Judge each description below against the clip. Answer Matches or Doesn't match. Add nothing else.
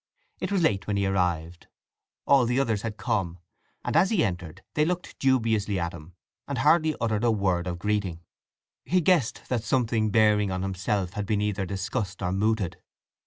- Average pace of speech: Matches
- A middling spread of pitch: Matches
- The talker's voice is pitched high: Doesn't match